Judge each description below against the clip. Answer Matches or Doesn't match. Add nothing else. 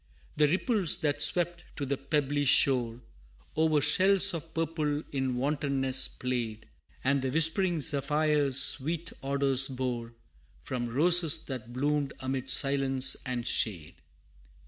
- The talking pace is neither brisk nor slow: Doesn't match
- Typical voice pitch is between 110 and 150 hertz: Matches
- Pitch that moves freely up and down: Doesn't match